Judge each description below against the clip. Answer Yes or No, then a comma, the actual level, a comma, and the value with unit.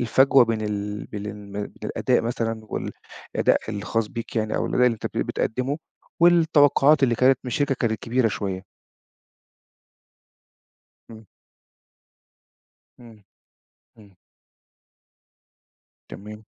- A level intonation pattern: No, average, 3.6 semitones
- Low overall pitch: Yes, low, 115 Hz